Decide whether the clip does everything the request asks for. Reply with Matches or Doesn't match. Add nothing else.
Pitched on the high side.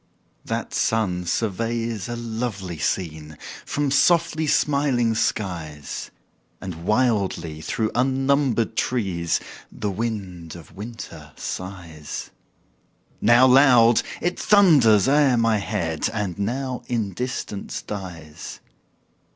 Doesn't match